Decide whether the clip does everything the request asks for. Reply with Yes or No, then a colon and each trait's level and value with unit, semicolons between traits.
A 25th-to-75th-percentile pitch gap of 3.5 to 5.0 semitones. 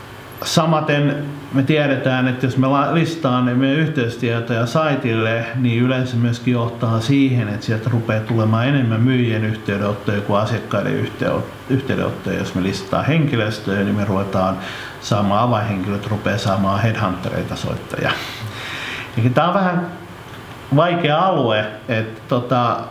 Yes: average, 4.1 semitones